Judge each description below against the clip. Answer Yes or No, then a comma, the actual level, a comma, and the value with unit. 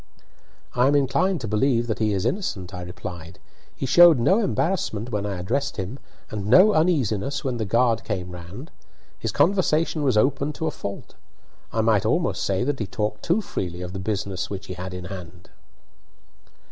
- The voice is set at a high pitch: No, low, 110 Hz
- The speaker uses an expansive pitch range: Yes, wide, 6.8 semitones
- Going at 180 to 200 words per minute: Yes, average, 185 wpm